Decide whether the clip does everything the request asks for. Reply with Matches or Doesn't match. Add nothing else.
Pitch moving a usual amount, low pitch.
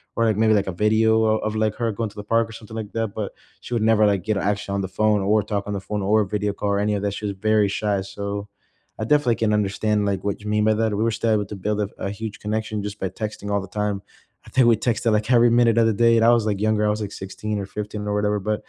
Doesn't match